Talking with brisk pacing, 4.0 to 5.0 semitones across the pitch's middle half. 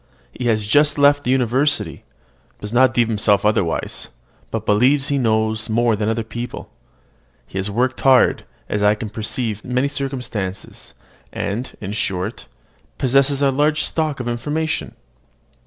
No: average, 150 wpm; average, 4.3 semitones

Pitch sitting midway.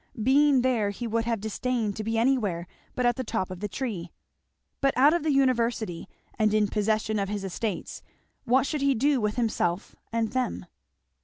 No: high, 230 Hz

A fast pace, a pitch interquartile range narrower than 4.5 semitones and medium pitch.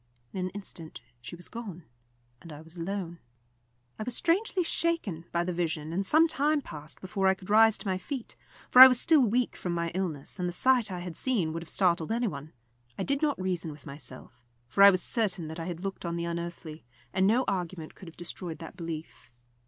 No: fast, 220 wpm; average, 5.0 semitones; medium, 180 Hz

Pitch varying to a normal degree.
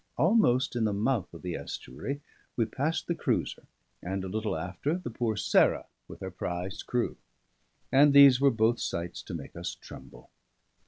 No: wide, 6.7 semitones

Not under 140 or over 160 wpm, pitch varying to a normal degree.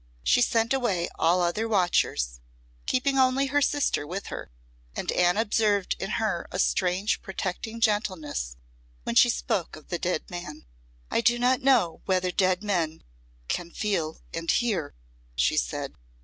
Yes: average, 150 wpm; average, 5.0 semitones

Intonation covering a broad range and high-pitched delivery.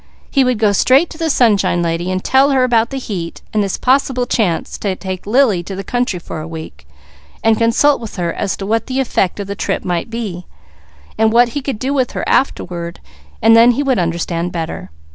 Yes: wide, 6.1 semitones; high, 220 Hz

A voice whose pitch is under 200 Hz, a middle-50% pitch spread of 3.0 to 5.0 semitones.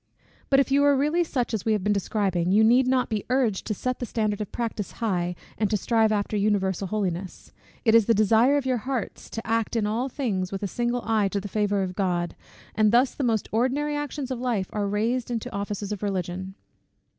No: high, 215 Hz; average, 3.7 semitones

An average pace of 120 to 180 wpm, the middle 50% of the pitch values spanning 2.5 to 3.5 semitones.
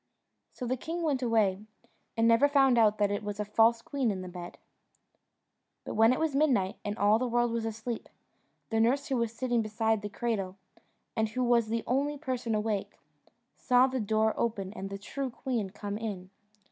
No: average, 195 wpm; average, 3.2 semitones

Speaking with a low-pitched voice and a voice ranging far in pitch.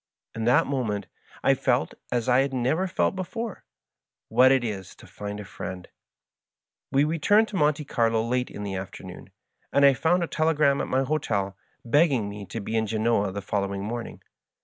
Yes: low, 120 Hz; wide, 6.2 semitones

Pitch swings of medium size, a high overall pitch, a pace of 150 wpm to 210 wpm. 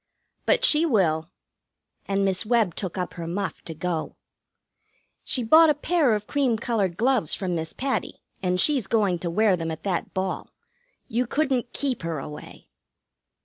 No: wide, 6.1 semitones; high, 200 Hz; average, 170 wpm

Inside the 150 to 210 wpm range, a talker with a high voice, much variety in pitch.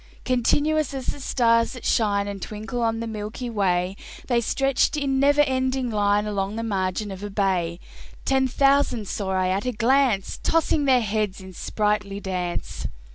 No: average, 170 wpm; high, 220 Hz; average, 4.7 semitones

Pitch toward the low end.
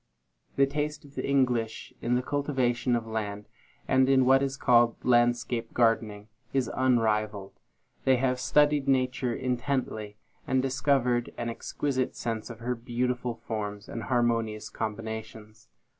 Yes: low, 120 Hz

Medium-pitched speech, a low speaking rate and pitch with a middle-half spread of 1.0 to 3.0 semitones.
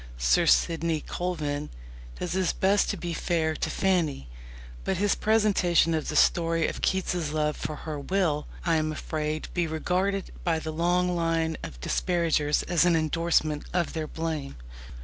No: medium, 165 Hz; average, 165 wpm; narrow, 2.5 semitones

